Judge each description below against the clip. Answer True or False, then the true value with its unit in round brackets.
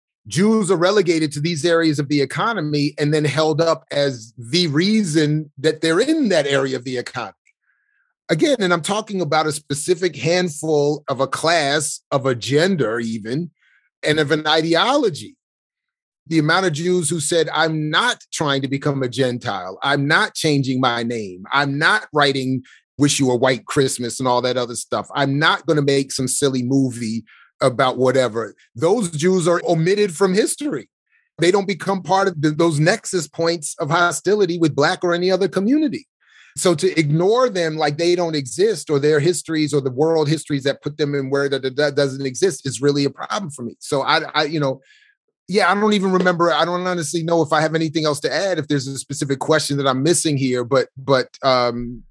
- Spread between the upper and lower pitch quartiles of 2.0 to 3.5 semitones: False (4.3 semitones)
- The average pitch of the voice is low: False (155 Hz)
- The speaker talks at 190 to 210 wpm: True (195 wpm)